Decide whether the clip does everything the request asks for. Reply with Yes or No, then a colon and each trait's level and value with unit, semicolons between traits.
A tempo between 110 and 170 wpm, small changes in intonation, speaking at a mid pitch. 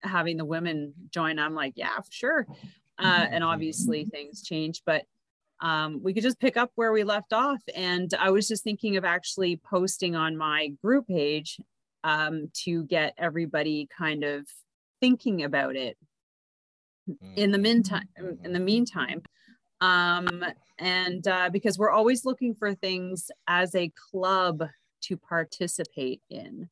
No: average, 150 wpm; average, 4.3 semitones; medium, 180 Hz